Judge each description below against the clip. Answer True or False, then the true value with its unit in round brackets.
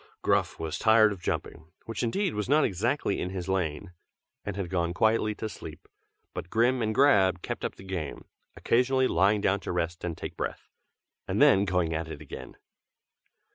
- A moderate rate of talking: True (180 wpm)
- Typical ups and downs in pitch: True (4.2 semitones)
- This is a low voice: True (95 Hz)